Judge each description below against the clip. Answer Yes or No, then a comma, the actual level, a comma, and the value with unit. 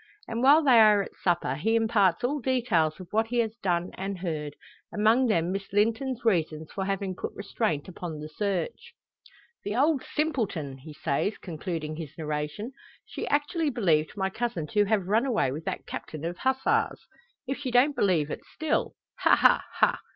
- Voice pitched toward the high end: Yes, high, 200 Hz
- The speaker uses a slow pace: No, average, 180 wpm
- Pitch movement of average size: No, wide, 6.7 semitones